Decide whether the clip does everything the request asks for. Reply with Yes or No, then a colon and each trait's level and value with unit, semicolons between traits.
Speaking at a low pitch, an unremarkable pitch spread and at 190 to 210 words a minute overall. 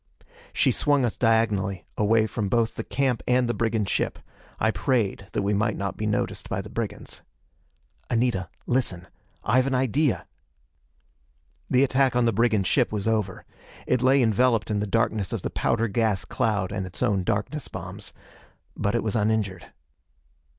No: low, 110 Hz; average, 3.3 semitones; average, 165 wpm